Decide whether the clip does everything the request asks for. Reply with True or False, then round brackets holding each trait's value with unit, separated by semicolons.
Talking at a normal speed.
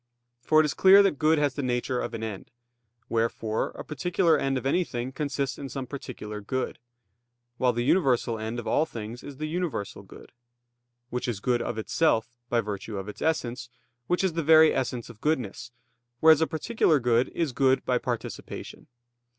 True (185 wpm)